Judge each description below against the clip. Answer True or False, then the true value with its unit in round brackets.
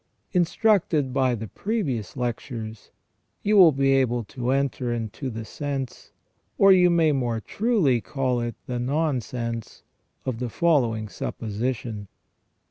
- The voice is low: True (130 Hz)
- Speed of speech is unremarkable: False (125 wpm)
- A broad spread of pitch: False (4.4 semitones)